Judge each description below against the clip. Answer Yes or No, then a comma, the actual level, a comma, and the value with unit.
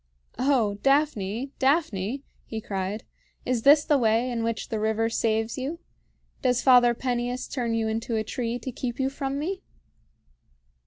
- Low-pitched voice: No, high, 240 Hz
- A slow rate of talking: No, average, 155 wpm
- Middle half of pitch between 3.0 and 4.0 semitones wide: Yes, average, 3.3 semitones